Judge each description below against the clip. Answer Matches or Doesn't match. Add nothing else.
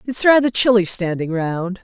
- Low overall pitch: Doesn't match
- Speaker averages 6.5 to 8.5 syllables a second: Doesn't match